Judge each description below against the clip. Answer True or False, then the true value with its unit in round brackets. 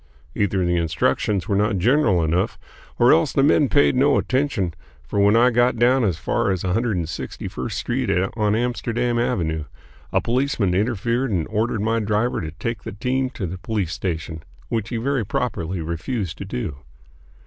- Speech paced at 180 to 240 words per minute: False (170 wpm)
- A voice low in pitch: True (110 Hz)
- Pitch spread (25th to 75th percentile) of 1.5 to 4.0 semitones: False (5.1 semitones)